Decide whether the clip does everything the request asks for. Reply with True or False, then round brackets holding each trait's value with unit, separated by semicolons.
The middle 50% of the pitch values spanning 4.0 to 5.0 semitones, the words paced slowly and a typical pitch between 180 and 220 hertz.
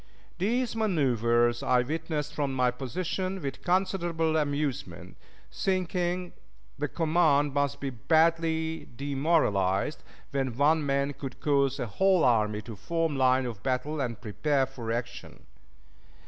False (4.6 semitones; 125 wpm; 145 Hz)